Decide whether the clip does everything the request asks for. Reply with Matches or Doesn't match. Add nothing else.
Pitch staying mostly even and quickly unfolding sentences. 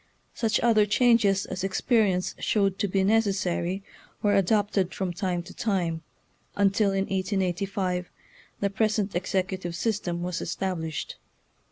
Doesn't match